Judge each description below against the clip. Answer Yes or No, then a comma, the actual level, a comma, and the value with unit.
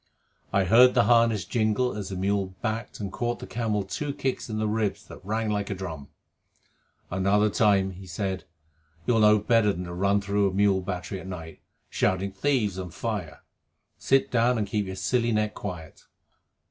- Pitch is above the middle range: No, low, 100 Hz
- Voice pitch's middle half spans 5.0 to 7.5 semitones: No, average, 3.0 semitones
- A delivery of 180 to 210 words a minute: Yes, average, 185 wpm